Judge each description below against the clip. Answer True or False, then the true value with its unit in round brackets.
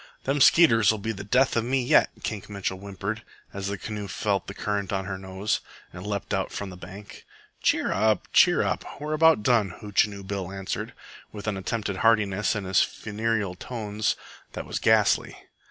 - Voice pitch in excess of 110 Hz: False (105 Hz)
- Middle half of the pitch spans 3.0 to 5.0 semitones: False (2.4 semitones)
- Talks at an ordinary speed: True (180 wpm)